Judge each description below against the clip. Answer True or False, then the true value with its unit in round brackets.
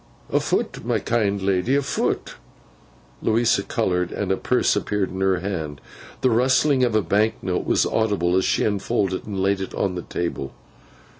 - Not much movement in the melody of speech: False (3.1 semitones)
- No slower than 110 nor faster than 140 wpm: False (170 wpm)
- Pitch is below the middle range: True (100 Hz)